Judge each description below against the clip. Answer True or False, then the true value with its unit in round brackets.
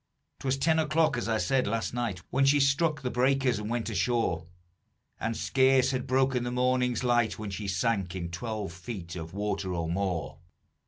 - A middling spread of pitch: True (5.0 semitones)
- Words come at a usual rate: True (180 wpm)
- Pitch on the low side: True (120 Hz)